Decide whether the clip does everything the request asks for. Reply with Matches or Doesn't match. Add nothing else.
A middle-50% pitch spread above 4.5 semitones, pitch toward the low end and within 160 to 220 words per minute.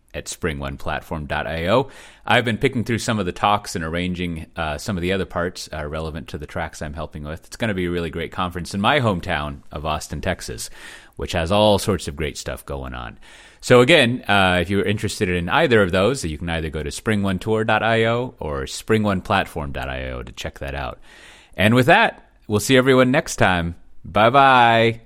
Matches